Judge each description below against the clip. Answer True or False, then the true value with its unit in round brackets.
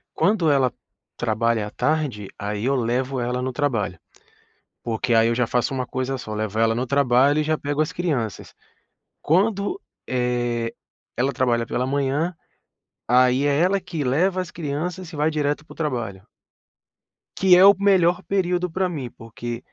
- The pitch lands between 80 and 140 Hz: True (135 Hz)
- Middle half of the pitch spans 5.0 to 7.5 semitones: True (5.3 semitones)